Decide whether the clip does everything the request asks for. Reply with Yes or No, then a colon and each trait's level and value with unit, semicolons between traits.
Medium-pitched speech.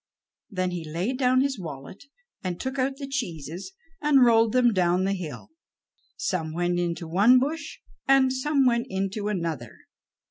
No: high, 200 Hz